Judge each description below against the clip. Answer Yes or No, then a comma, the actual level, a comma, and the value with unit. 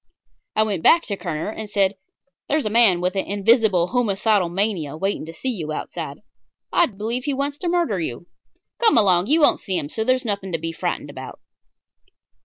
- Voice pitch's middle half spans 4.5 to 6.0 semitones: Yes, average, 5.1 semitones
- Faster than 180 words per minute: Yes, average, 195 wpm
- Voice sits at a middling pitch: No, high, 205 Hz